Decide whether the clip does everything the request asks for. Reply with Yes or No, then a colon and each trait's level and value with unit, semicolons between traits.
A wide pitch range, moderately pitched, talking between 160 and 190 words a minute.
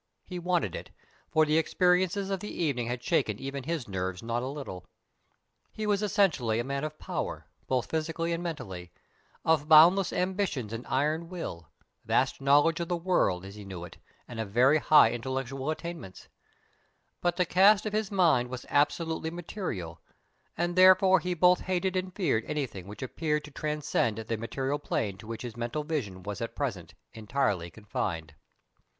Yes: wide, 7.4 semitones; medium, 150 Hz; average, 170 wpm